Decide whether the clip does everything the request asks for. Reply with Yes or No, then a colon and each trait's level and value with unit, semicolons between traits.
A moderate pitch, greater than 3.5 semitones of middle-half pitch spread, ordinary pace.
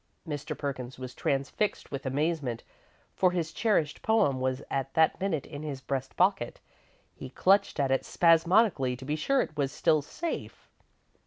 Yes: medium, 145 Hz; average, 4.4 semitones; average, 160 wpm